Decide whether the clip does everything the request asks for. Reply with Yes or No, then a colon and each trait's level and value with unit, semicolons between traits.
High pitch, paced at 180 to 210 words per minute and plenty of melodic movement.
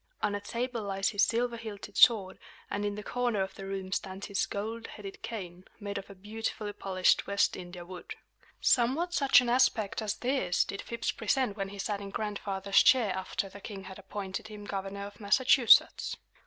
No: high, 205 Hz; average, 190 wpm; average, 2.8 semitones